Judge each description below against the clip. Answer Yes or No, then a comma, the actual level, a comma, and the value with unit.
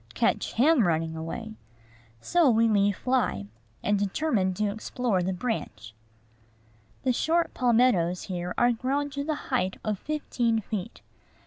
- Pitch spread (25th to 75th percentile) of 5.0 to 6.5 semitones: Yes, wide, 5.4 semitones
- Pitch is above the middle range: Yes, high, 220 Hz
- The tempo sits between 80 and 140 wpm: Yes, slow, 135 wpm